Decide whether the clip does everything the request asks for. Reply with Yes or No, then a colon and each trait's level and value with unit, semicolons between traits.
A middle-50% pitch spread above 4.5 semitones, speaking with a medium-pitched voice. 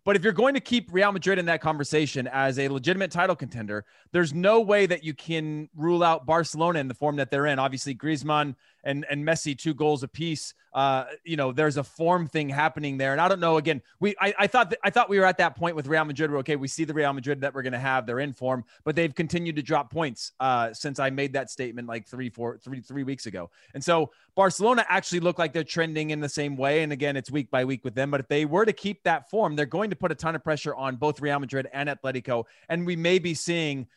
No: average, 3.8 semitones; medium, 150 Hz